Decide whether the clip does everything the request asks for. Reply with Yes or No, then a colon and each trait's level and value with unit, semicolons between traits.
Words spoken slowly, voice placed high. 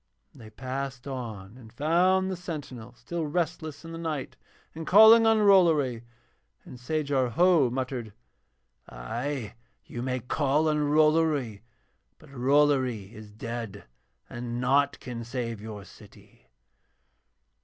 No: slow, 125 wpm; low, 135 Hz